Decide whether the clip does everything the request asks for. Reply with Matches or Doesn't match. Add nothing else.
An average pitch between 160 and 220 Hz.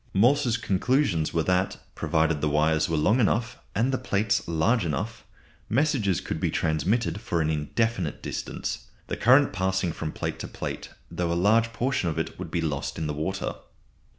Doesn't match